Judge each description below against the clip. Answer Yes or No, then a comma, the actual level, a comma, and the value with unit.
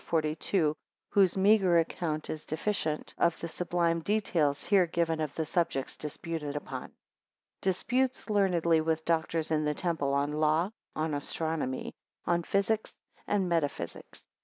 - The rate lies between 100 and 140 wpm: No, average, 155 wpm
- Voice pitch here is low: No, medium, 165 Hz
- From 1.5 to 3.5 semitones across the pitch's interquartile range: Yes, average, 2.8 semitones